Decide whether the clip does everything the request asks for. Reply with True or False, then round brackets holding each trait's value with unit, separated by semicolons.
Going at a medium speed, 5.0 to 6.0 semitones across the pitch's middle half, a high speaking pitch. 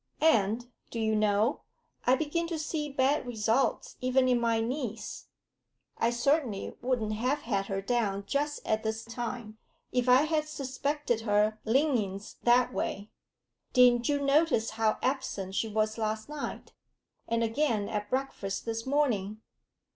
False (145 wpm; 4.0 semitones; 235 Hz)